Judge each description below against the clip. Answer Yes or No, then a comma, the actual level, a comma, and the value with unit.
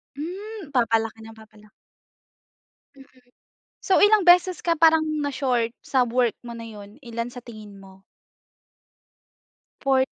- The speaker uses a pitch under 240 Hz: No, high, 245 Hz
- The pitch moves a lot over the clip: Yes, wide, 6.1 semitones